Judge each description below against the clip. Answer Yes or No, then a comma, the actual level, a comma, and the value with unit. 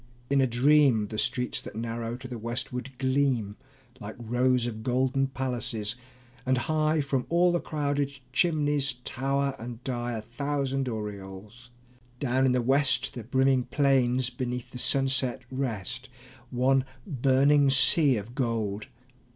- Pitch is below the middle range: Yes, low, 130 Hz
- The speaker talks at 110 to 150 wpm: Yes, average, 140 wpm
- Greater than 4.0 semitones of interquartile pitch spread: No, narrow, 2.5 semitones